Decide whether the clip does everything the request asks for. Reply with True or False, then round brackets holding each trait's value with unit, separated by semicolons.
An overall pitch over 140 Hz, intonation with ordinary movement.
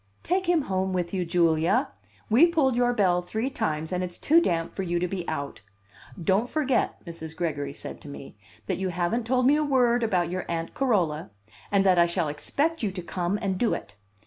False (185 Hz; 6.3 semitones)